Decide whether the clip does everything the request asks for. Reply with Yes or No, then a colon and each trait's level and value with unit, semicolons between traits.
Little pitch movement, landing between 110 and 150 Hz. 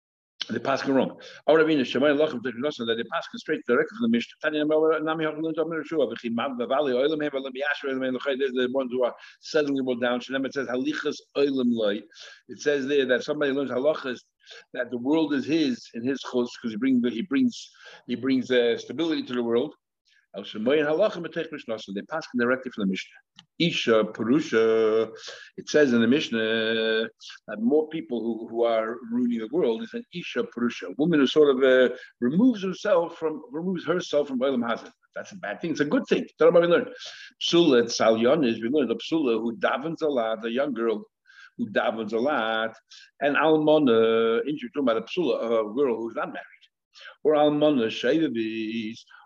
No: average, 5.2 semitones; low, 135 Hz